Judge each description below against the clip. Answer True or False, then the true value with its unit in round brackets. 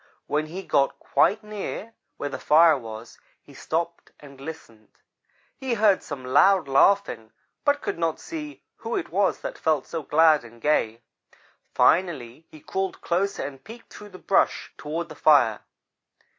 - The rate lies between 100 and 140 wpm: False (155 wpm)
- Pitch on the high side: False (160 Hz)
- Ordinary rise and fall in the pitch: False (5.9 semitones)